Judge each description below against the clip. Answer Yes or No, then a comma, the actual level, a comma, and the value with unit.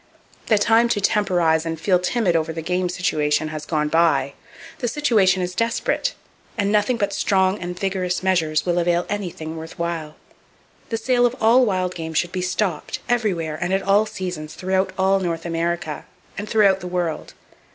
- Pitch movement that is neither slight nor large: Yes, average, 3.7 semitones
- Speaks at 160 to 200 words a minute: Yes, average, 175 wpm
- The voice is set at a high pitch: No, medium, 180 Hz